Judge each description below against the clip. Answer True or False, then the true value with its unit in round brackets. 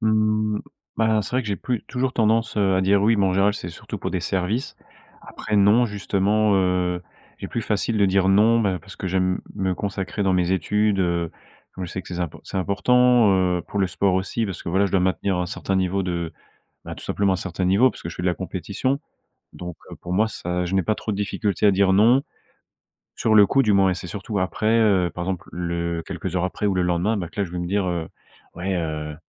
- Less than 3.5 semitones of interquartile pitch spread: True (2.8 semitones)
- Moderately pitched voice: False (95 Hz)